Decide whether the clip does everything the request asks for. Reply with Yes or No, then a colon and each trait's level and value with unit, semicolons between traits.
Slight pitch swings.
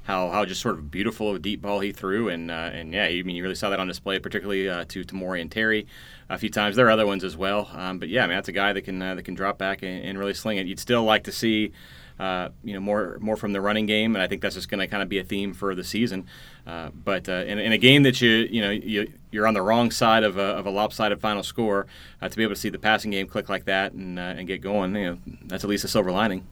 Yes: narrow, 2.3 semitones